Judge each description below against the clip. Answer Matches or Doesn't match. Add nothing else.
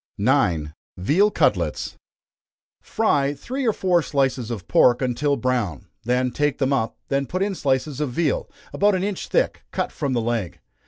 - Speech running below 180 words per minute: Matches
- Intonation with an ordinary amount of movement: Doesn't match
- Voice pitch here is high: Doesn't match